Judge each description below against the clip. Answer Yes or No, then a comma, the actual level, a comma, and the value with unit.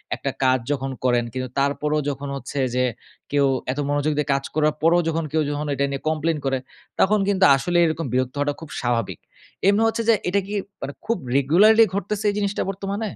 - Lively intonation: Yes, wide, 6.1 semitones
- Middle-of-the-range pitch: Yes, medium, 150 Hz